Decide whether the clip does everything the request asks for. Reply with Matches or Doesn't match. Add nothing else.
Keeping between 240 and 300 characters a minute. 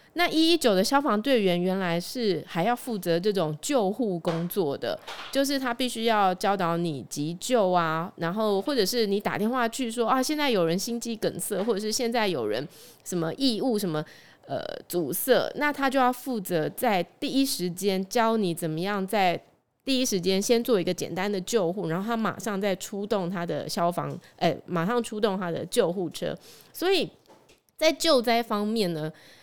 Matches